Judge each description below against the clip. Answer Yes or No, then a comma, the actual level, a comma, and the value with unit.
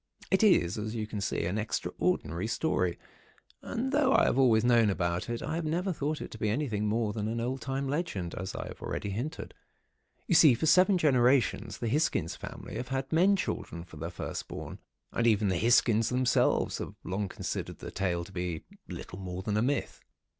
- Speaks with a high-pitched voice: No, low, 115 Hz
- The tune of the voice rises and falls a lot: Yes, wide, 6.8 semitones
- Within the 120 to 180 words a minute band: No, average, 200 wpm